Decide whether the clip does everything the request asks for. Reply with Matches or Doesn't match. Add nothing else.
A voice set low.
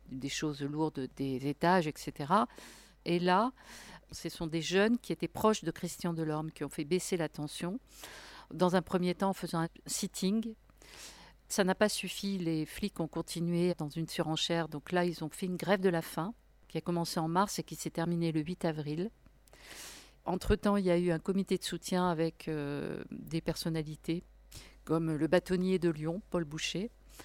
Doesn't match